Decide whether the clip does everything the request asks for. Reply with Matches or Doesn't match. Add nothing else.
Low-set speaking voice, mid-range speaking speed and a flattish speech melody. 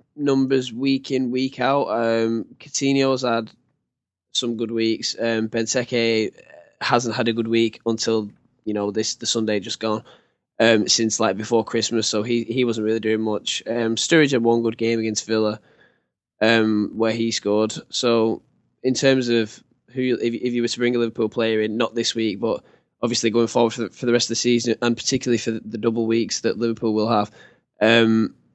Matches